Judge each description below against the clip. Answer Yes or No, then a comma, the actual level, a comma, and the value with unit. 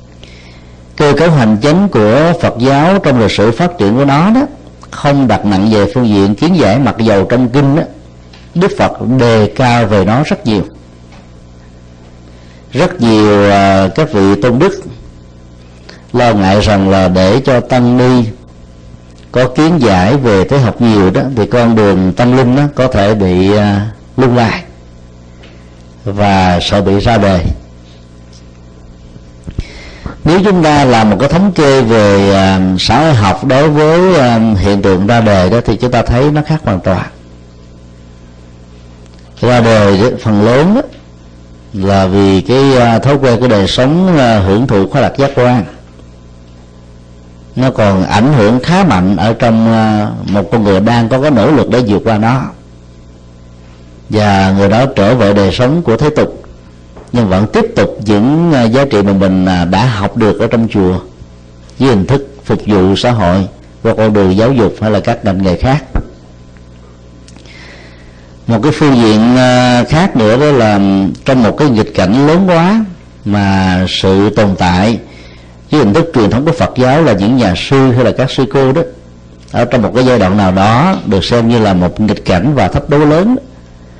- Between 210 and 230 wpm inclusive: No, average, 175 wpm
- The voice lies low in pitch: Yes, low, 100 Hz